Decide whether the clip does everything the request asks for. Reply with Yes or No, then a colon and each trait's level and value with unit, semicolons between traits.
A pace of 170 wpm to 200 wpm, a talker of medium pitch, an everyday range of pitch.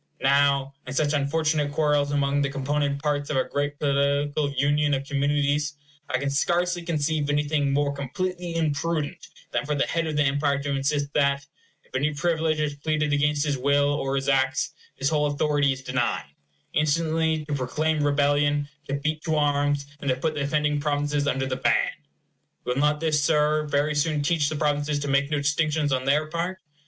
No: average, 185 wpm; medium, 145 Hz; narrow, 1.3 semitones